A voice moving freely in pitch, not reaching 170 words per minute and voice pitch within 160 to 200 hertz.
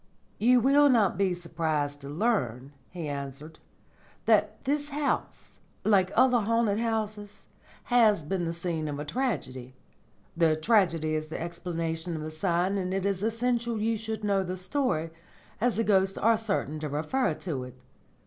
Yes: wide, 6.2 semitones; average, 160 wpm; medium, 185 Hz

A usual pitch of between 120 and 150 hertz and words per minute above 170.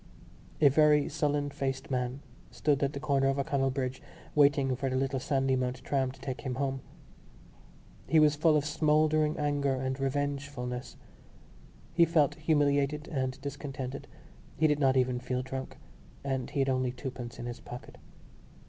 No: low, 135 Hz; average, 155 wpm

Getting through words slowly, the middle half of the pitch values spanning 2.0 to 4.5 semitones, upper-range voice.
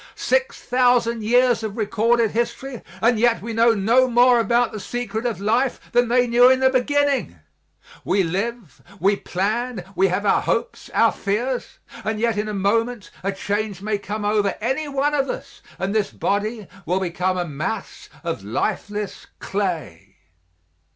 No: average, 160 wpm; average, 3.5 semitones; high, 220 Hz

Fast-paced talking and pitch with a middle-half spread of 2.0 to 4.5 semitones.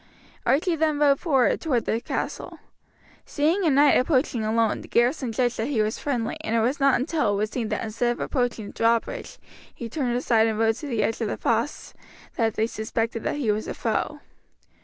Yes: fast, 210 wpm; average, 4.0 semitones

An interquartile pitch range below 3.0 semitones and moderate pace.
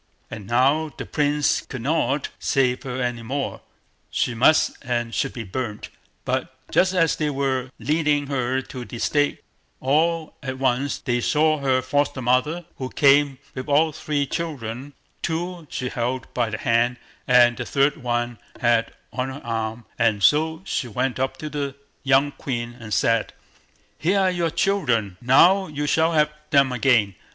No: average, 3.6 semitones; average, 160 wpm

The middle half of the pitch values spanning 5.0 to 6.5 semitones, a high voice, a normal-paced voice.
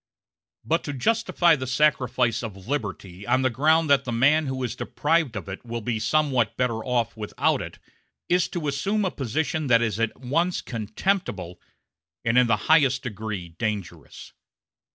No: wide, 5.4 semitones; low, 125 Hz; average, 165 wpm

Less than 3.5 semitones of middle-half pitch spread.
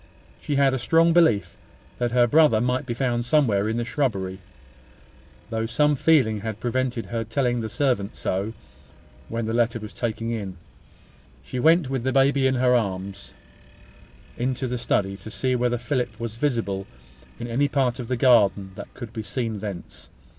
Yes: average, 3.1 semitones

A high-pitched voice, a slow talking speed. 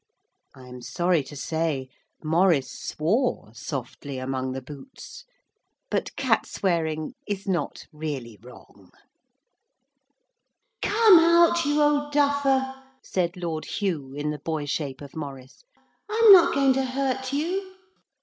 No: medium, 170 Hz; slow, 125 wpm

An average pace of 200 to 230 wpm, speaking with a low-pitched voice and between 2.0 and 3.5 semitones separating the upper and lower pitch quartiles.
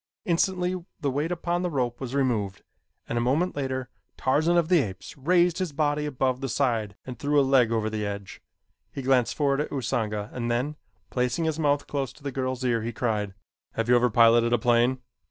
No: fast, 205 wpm; low, 130 Hz; average, 3.9 semitones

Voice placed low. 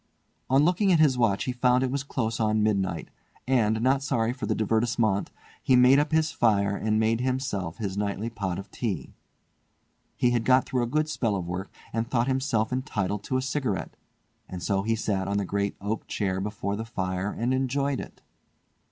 Yes: low, 115 Hz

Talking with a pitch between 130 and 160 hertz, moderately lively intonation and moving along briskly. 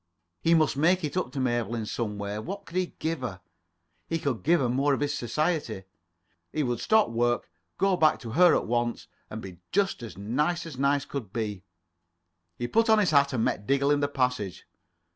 No: medium, 140 Hz; wide, 5.8 semitones; fast, 215 wpm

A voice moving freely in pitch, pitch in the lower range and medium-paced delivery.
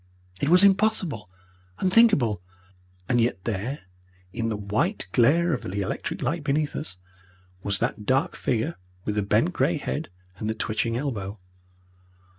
Yes: wide, 6.9 semitones; low, 120 Hz; average, 145 wpm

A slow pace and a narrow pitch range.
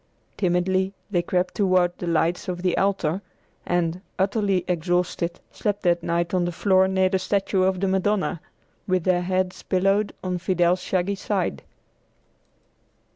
No: average, 145 wpm; narrow, 1.3 semitones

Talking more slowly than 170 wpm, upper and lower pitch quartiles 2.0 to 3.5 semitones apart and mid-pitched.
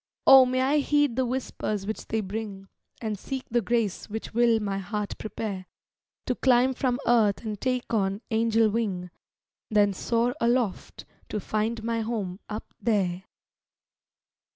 No: average, 150 wpm; average, 2.8 semitones; high, 225 Hz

